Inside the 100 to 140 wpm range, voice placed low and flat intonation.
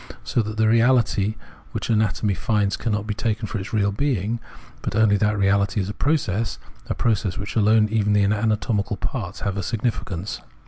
No: average, 190 wpm; low, 105 Hz; narrow, 2.0 semitones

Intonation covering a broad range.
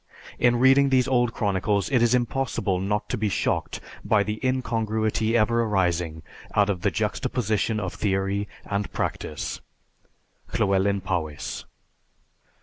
No: average, 3.4 semitones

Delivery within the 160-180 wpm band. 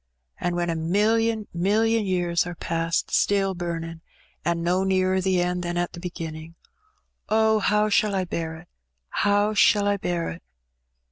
Yes: average, 165 wpm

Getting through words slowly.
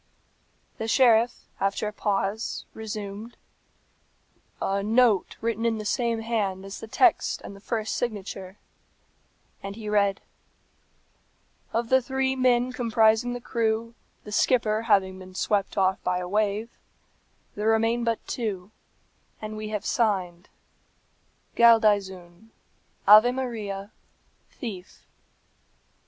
Yes: slow, 115 wpm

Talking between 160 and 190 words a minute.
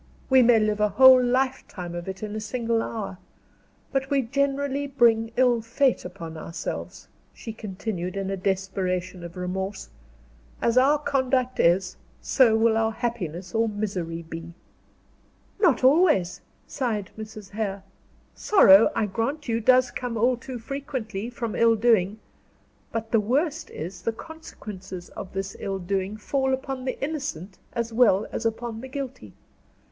No: average, 150 wpm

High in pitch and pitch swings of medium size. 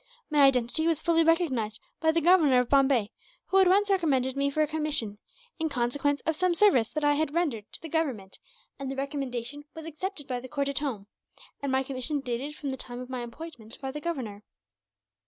Yes: very high, 280 Hz; average, 4.2 semitones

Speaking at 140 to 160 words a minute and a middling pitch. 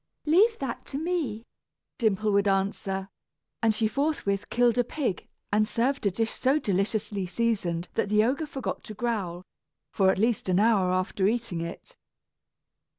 No: average, 155 wpm; high, 215 Hz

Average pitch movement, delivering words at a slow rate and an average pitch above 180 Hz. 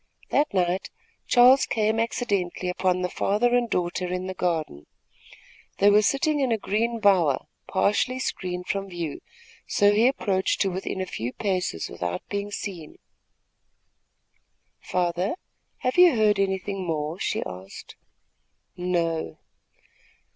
Yes: average, 3.4 semitones; slow, 130 wpm; high, 190 Hz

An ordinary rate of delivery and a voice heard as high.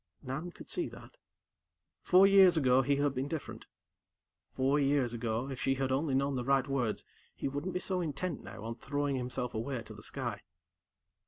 No: average, 185 wpm; low, 135 Hz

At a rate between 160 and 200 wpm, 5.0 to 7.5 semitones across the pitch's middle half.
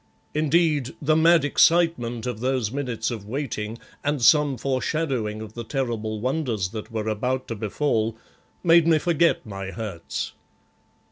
No: average, 140 wpm; wide, 5.4 semitones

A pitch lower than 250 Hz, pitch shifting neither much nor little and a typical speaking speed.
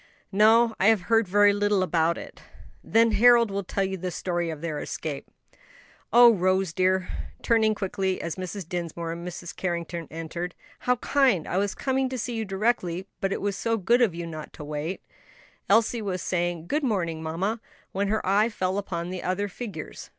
Yes: high, 190 Hz; average, 4.1 semitones; average, 185 wpm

